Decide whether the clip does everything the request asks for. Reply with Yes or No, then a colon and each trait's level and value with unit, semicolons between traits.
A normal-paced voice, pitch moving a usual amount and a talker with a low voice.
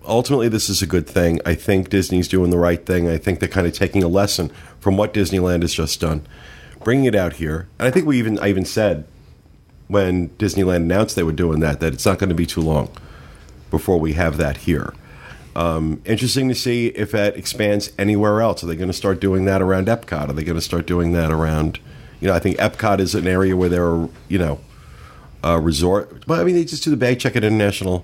No: fast, 230 wpm; average, 3.8 semitones; very low, 90 Hz